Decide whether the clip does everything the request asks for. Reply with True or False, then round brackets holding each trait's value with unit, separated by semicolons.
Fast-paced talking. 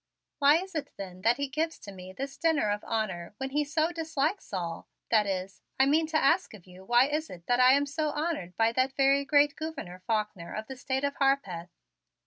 True (220 wpm)